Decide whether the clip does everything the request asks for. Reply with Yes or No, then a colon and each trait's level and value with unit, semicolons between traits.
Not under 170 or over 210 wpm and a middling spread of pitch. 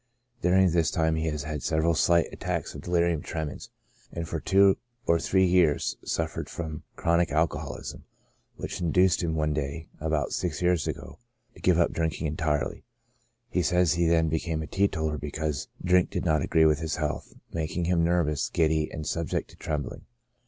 No: average, 175 wpm; narrow, 1.9 semitones